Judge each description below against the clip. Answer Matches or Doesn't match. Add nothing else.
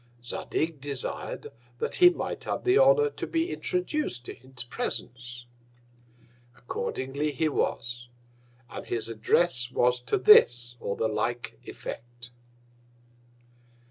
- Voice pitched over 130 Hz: Doesn't match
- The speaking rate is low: Matches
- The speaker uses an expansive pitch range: Matches